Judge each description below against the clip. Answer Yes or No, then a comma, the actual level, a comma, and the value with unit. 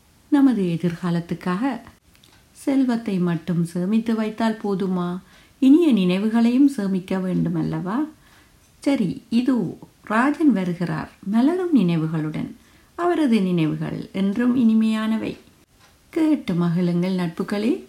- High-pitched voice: Yes, high, 210 Hz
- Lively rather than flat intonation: Yes, wide, 6.7 semitones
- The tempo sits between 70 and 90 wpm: Yes, average, 85 wpm